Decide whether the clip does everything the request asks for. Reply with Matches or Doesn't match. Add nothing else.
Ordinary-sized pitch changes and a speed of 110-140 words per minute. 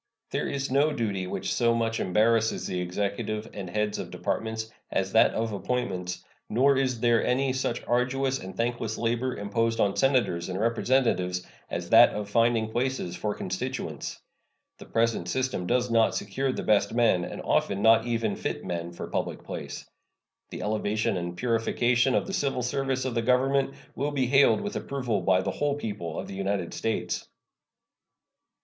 Doesn't match